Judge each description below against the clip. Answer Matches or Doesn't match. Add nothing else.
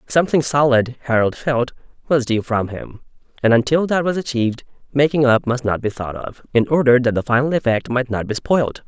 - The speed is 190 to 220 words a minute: Matches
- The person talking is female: Doesn't match